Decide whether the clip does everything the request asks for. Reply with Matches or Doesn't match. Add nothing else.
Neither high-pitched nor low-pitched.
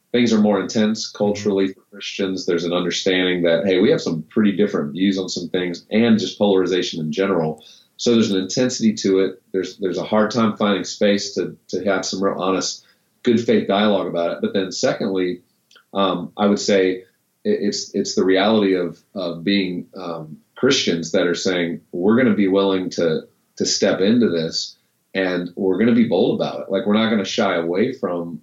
Doesn't match